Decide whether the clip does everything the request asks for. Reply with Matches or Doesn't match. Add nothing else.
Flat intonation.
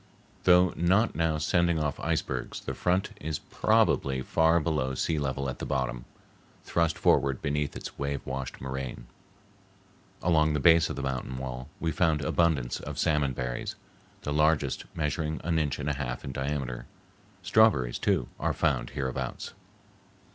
Doesn't match